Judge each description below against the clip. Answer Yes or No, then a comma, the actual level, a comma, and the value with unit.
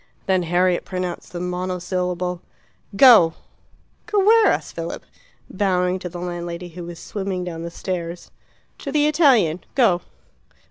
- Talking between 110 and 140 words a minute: Yes, slow, 135 wpm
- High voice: No, medium, 180 Hz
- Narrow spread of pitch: Yes, narrow, 2.2 semitones